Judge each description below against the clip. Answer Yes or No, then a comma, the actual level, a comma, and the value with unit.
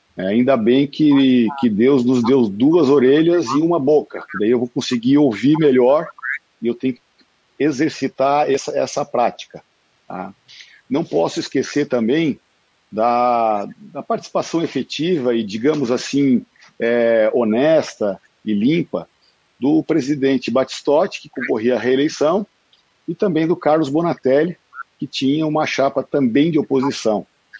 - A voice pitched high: No, low, 135 Hz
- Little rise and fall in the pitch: No, average, 3.6 semitones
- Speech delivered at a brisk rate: No, average, 135 wpm